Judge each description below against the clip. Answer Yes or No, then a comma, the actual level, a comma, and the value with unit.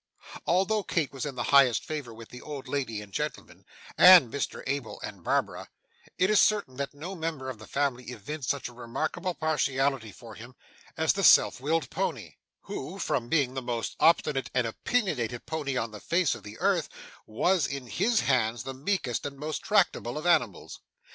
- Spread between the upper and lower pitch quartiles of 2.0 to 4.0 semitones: No, average, 4.7 semitones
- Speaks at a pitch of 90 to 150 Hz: Yes, low, 135 Hz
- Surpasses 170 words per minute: Yes, average, 185 wpm